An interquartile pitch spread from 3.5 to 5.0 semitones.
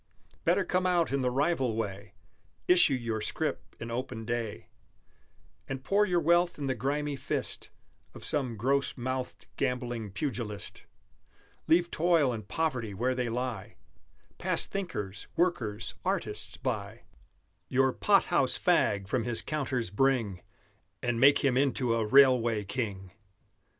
Yes: average, 4.0 semitones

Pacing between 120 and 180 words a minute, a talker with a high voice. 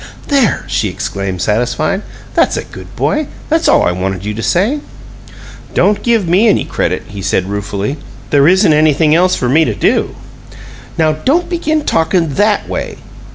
No: average, 165 wpm; medium, 160 Hz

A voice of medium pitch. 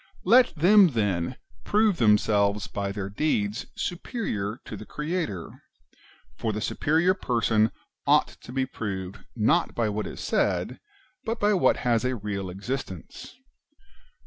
No: low, 110 Hz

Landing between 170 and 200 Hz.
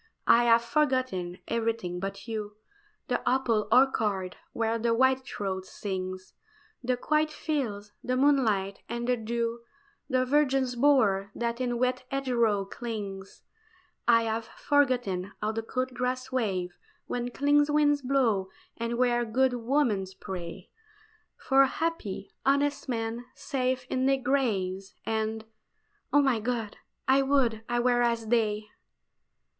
No: high, 235 Hz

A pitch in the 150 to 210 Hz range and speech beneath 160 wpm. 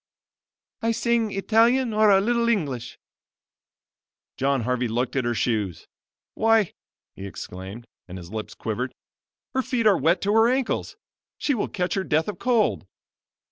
Yes: high, 190 Hz; average, 150 wpm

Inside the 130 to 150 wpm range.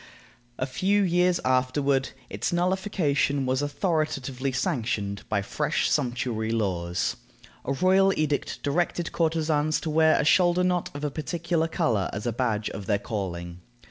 Yes: average, 140 wpm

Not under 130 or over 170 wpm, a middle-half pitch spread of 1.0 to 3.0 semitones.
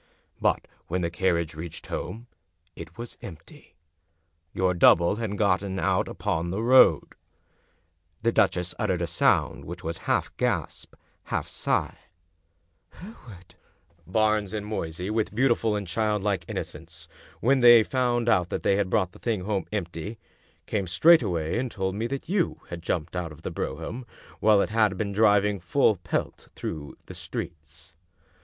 No: average, 155 wpm; average, 4.3 semitones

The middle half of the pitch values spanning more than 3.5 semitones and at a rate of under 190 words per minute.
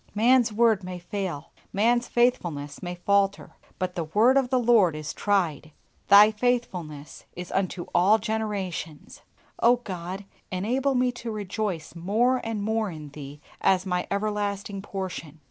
Yes: average, 4.1 semitones; average, 145 wpm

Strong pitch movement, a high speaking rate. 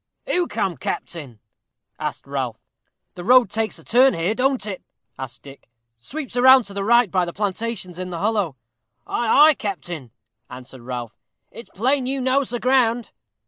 No: wide, 6.6 semitones; average, 165 wpm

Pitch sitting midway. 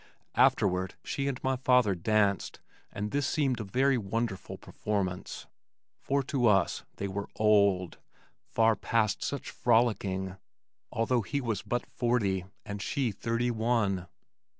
No: low, 110 Hz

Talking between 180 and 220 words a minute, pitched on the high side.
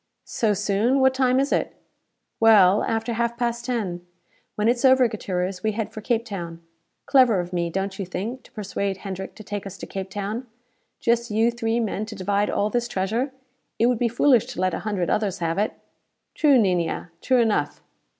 Yes: average, 195 wpm; high, 215 Hz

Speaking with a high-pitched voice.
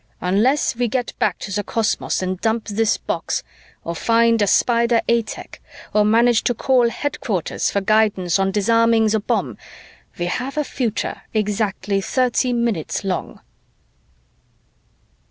Yes: high, 220 Hz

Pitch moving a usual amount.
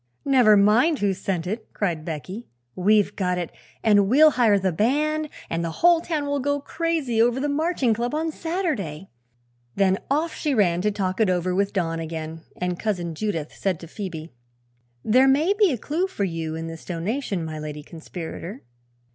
No: wide, 8.4 semitones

